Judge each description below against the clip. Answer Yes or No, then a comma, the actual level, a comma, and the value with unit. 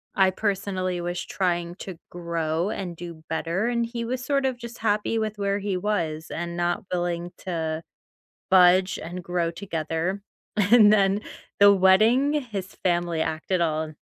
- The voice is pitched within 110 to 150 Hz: No, medium, 185 Hz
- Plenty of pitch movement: No, average, 3.3 semitones